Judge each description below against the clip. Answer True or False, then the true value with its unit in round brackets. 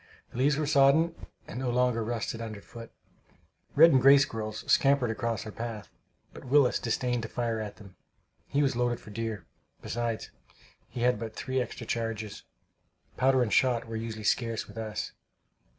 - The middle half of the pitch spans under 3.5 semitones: True (2.6 semitones)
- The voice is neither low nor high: False (115 Hz)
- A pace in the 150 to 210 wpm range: True (165 wpm)